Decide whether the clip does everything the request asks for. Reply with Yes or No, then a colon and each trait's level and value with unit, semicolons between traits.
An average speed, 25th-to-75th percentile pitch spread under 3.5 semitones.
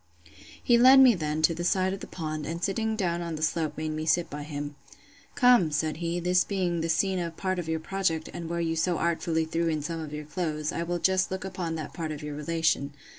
No: fast, 245 wpm; average, 2.8 semitones